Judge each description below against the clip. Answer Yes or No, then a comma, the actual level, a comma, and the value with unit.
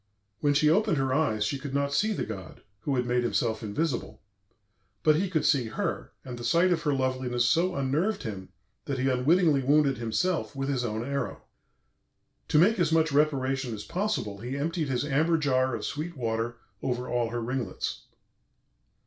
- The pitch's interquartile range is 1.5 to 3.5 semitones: No, average, 4.2 semitones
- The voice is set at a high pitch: No, low, 135 Hz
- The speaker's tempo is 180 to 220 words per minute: Yes, average, 185 wpm